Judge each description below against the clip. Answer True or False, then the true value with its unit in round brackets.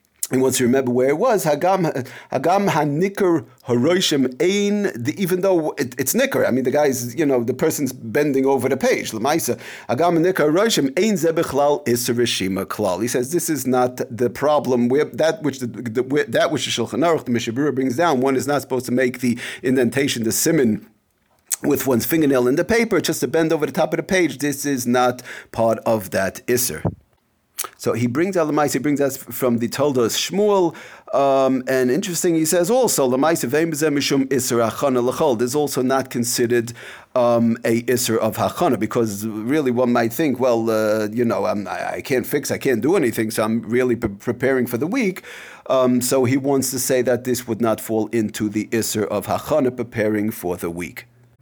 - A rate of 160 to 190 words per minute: True (185 wpm)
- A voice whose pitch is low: True (130 Hz)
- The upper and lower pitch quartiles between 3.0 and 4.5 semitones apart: True (3.9 semitones)